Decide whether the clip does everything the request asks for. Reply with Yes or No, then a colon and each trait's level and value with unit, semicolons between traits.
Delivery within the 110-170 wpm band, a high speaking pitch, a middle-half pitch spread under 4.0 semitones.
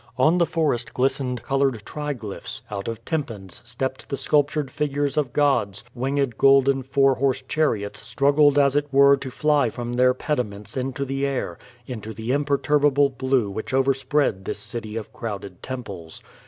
No: average, 160 wpm; low, 135 Hz; average, 3.6 semitones